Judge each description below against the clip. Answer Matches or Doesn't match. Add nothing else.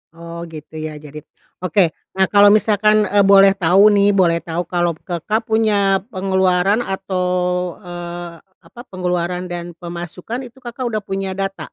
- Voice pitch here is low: Doesn't match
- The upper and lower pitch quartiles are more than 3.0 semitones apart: Doesn't match